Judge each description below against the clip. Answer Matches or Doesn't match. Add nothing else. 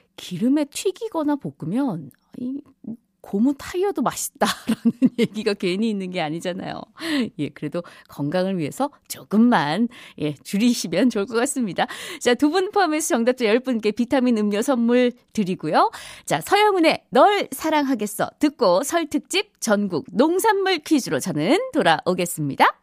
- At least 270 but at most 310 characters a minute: Matches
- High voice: Matches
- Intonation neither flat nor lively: Doesn't match